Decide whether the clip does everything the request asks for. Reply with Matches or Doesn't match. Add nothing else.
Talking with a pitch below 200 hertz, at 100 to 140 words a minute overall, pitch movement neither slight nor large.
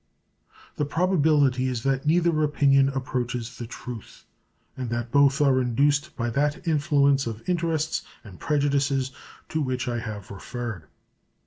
Matches